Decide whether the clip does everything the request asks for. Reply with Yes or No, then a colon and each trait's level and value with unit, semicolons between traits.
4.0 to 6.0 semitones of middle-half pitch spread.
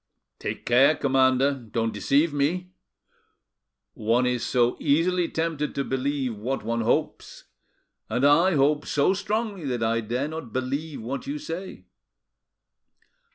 Yes: average, 4.6 semitones